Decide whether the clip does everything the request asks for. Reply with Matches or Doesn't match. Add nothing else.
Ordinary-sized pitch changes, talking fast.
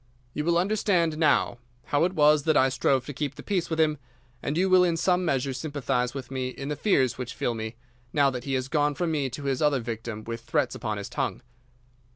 Matches